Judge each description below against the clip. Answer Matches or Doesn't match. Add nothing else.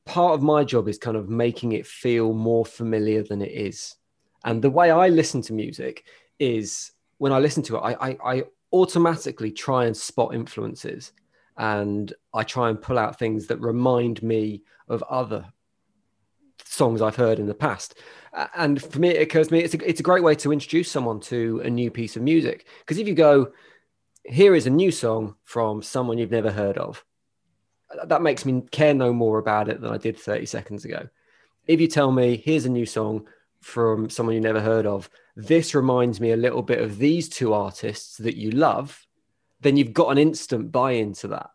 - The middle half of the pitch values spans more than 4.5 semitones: Matches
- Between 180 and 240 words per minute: Matches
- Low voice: Matches